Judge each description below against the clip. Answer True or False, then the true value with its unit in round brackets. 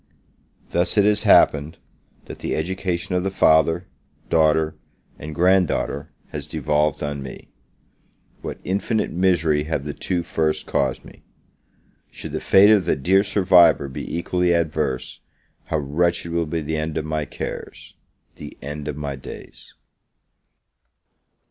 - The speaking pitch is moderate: False (80 Hz)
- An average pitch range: True (3.1 semitones)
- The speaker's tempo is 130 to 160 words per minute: True (140 wpm)